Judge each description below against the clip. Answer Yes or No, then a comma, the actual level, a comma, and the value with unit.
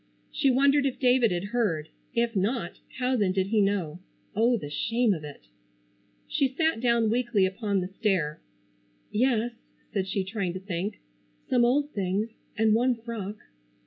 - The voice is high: Yes, high, 220 Hz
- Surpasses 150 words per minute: Yes, average, 160 wpm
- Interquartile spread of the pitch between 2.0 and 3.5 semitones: No, average, 4.3 semitones